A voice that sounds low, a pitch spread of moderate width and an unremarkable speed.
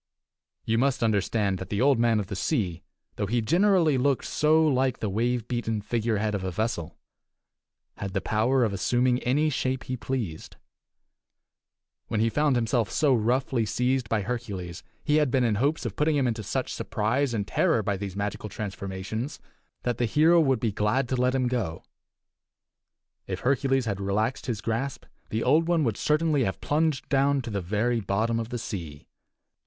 Yes: low, 120 Hz; average, 4.3 semitones; average, 180 wpm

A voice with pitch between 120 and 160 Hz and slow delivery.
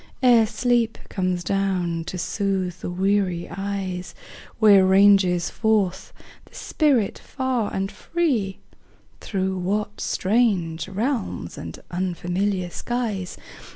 No: high, 195 Hz; slow, 105 wpm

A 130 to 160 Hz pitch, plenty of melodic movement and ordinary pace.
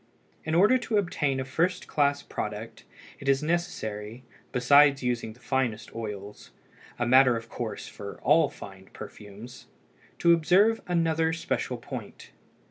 No: low, 135 Hz; wide, 6.1 semitones; slow, 130 wpm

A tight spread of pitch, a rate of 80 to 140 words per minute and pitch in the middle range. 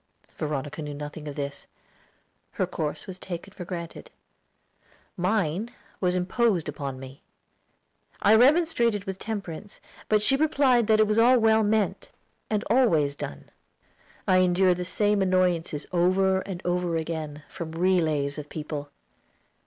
No: wide, 5.4 semitones; slow, 135 wpm; medium, 180 Hz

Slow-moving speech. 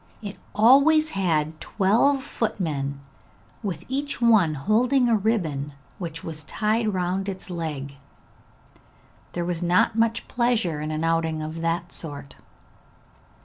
Yes: slow, 125 wpm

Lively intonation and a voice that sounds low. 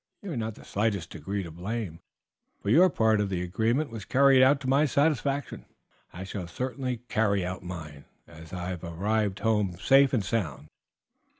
Yes: wide, 6.3 semitones; low, 105 Hz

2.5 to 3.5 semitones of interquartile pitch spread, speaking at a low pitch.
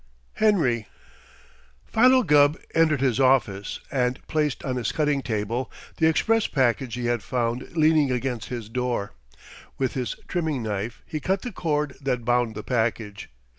No: average, 4.4 semitones; low, 130 Hz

